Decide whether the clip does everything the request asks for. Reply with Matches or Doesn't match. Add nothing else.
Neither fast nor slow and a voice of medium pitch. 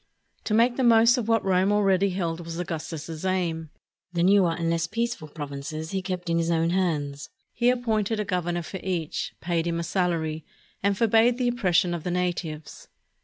Matches